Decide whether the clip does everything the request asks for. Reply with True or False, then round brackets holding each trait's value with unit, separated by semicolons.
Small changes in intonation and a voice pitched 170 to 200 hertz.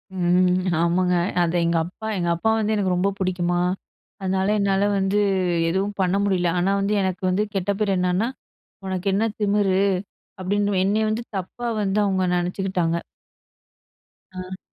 True (1.9 semitones; 190 Hz)